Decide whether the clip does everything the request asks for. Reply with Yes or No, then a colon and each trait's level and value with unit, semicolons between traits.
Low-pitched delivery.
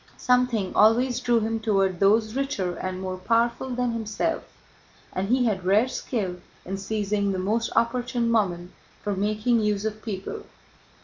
No: high, 215 Hz